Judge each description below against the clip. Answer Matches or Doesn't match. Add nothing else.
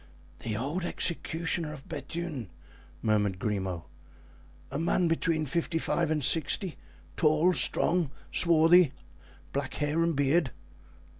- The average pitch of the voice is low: Doesn't match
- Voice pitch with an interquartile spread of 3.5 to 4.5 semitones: Matches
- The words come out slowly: Matches